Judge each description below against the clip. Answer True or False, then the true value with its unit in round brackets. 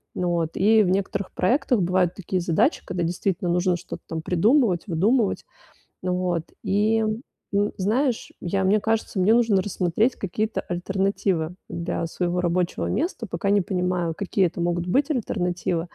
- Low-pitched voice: False (185 Hz)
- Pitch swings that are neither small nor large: True (3.2 semitones)